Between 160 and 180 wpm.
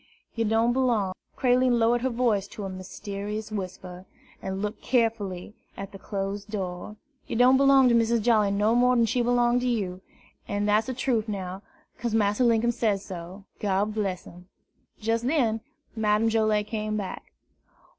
Yes: average, 170 wpm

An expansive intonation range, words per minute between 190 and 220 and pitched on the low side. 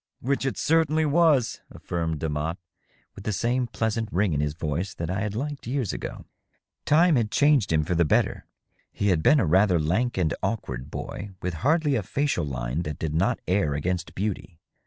Yes: wide, 7.8 semitones; average, 195 wpm; low, 100 Hz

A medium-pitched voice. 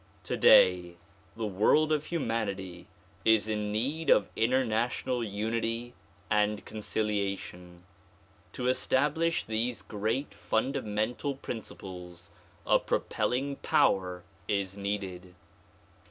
No: low, 110 Hz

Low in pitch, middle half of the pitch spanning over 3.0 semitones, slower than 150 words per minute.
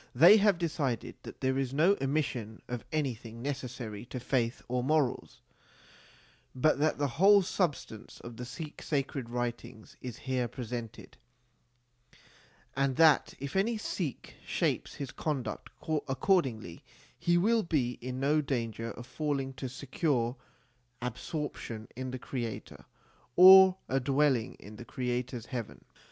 Yes: low, 130 Hz; average, 4.1 semitones; average, 140 wpm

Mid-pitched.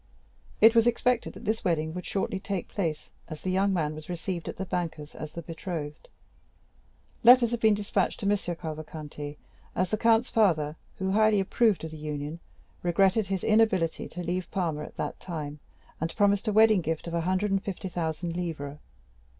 Yes: medium, 180 Hz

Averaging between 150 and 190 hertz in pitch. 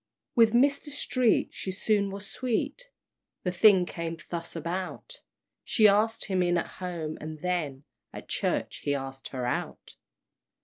Yes: medium, 185 Hz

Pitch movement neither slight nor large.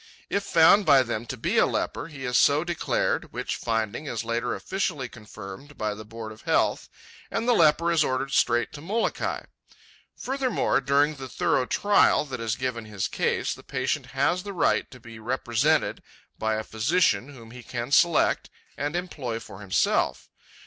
No: wide, 5.9 semitones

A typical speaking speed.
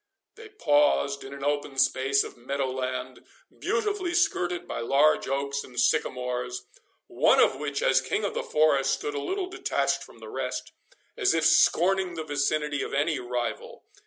Yes: average, 165 wpm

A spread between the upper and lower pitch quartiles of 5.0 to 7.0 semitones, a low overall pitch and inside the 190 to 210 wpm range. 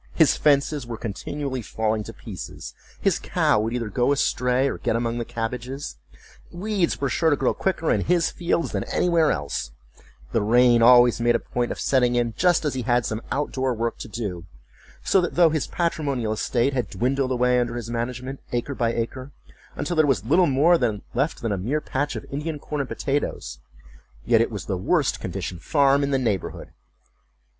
No: average, 3.8 semitones; low, 125 Hz; average, 195 wpm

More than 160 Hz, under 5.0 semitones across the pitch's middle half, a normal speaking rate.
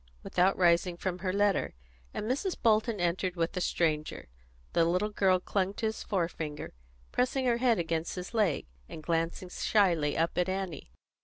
Yes: medium, 185 Hz; average, 3.5 semitones; average, 165 wpm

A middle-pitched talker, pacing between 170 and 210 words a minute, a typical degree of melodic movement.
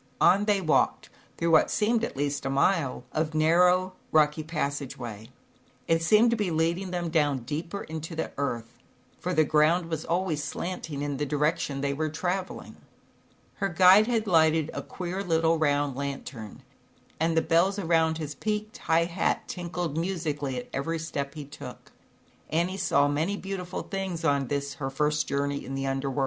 Yes: medium, 160 Hz; average, 175 wpm; average, 3.9 semitones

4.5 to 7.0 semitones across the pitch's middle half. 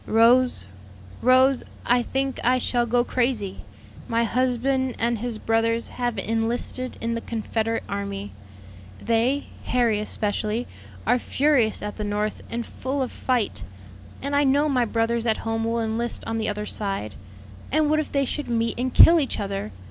No: narrow, 2.5 semitones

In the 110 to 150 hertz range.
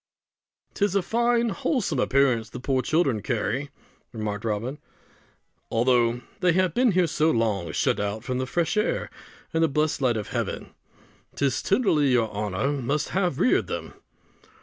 Yes: low, 135 Hz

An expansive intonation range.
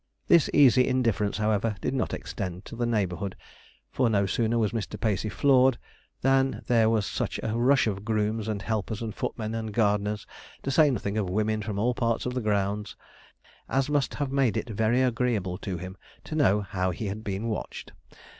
No: average, 3.3 semitones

